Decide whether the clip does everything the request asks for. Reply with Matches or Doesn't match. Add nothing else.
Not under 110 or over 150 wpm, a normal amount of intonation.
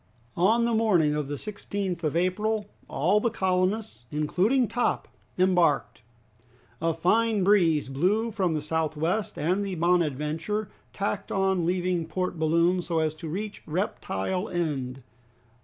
Matches